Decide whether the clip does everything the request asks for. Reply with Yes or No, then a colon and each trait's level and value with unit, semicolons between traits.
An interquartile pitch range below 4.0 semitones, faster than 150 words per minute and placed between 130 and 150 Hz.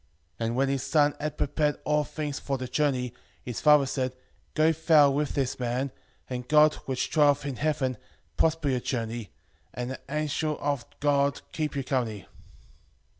Yes: average, 2.9 semitones; average, 165 wpm; medium, 140 Hz